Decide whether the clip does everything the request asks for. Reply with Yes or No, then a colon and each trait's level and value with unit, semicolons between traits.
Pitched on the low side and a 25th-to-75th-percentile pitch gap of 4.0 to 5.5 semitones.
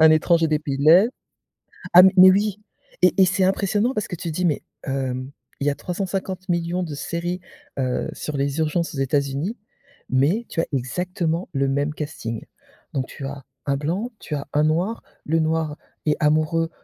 No: medium, 160 Hz; average, 4.3 semitones